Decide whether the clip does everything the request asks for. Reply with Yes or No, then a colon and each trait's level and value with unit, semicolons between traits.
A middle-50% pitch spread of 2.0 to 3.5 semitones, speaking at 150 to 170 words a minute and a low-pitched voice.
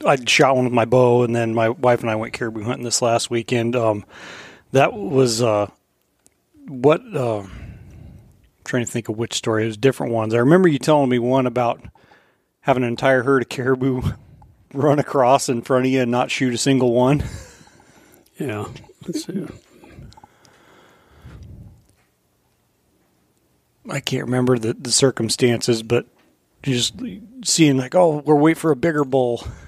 Yes: narrow, 2.6 semitones; average, 160 wpm; low, 125 Hz